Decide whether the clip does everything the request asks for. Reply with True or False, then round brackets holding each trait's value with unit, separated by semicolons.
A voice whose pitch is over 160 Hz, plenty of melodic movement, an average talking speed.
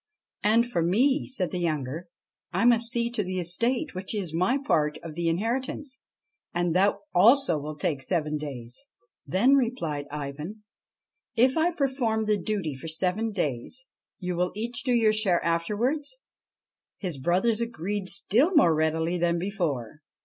True (190 Hz; 6.3 semitones; 170 wpm)